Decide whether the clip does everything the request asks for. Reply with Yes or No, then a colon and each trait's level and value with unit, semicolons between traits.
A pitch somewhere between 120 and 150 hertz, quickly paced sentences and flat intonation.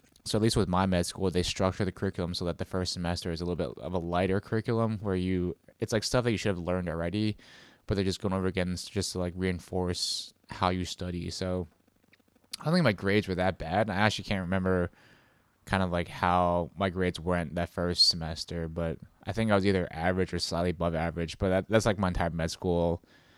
No: very low, 90 Hz; fast, 235 wpm; narrow, 2.2 semitones